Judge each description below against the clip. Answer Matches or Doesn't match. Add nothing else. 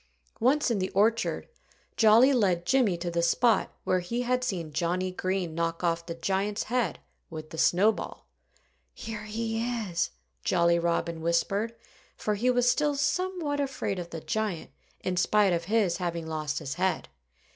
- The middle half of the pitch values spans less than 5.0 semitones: Doesn't match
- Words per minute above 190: Doesn't match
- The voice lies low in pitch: Doesn't match